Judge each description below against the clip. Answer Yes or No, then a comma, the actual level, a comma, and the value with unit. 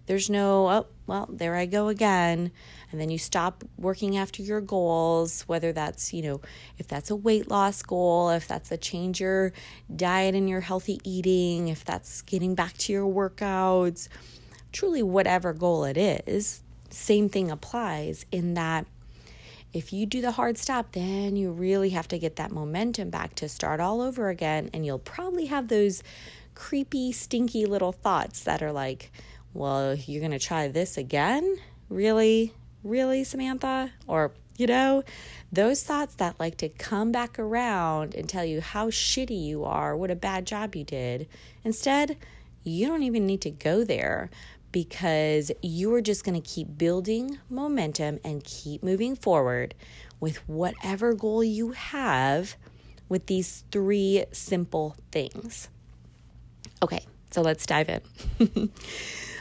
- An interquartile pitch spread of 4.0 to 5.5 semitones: Yes, average, 5.0 semitones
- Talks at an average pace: Yes, average, 155 wpm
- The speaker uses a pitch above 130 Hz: Yes, medium, 185 Hz